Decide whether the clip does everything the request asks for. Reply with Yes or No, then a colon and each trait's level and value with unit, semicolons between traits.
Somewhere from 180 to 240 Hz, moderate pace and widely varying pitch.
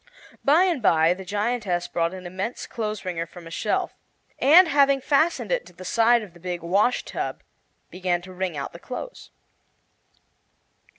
Yes: high, 190 Hz; average, 170 wpm; wide, 6.1 semitones